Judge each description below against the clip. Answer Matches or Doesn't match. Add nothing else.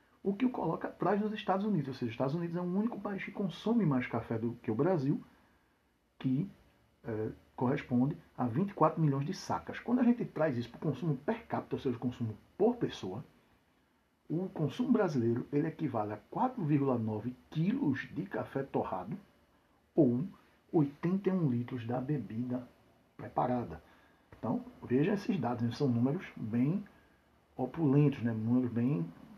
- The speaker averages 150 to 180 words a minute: Matches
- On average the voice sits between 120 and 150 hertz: Matches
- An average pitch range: Doesn't match